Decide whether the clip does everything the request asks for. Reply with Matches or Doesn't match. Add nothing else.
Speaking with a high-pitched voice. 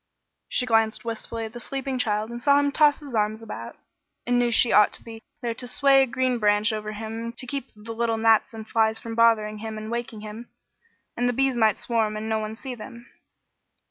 Matches